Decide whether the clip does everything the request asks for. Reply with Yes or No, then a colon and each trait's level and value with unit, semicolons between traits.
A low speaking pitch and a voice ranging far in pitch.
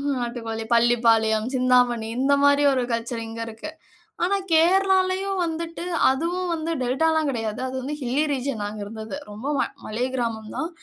No: very high, 255 Hz; wide, 5.9 semitones